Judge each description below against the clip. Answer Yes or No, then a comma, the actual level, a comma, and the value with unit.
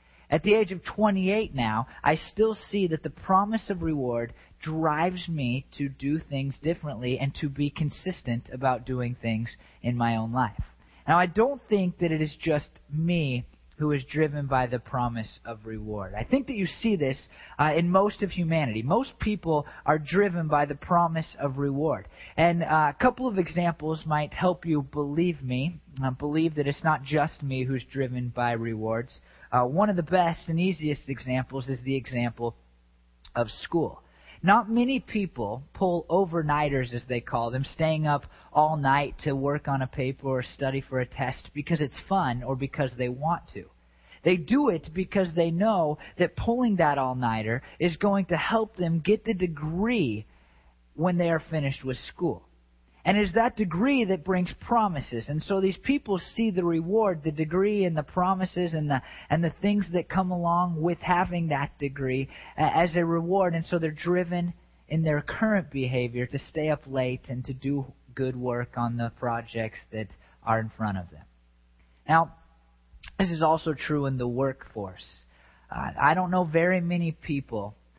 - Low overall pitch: No, medium, 150 Hz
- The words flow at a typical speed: Yes, average, 180 wpm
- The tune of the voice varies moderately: No, wide, 5.8 semitones